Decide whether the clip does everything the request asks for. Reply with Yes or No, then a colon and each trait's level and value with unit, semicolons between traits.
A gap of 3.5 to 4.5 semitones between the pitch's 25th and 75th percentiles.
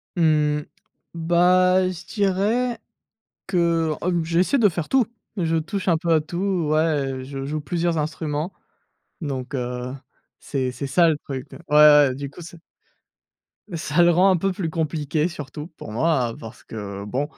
Yes: average, 3.8 semitones